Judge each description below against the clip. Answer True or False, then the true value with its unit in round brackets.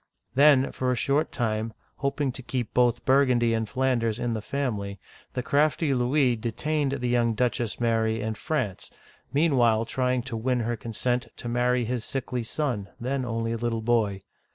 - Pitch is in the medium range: False (120 Hz)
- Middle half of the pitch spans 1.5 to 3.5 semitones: True (2.5 semitones)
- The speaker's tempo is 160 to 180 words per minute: True (175 wpm)